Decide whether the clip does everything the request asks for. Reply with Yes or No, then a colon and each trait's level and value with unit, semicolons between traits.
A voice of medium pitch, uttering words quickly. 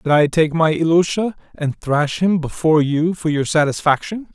No: medium, 160 Hz; average, 180 wpm